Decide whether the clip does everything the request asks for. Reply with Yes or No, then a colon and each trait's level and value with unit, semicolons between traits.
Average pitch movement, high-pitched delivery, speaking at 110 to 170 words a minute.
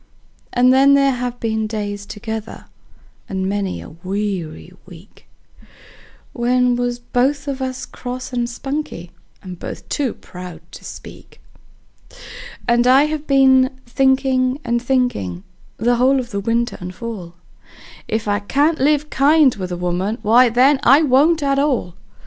Yes: average, 4.7 semitones; high, 245 Hz; average, 145 wpm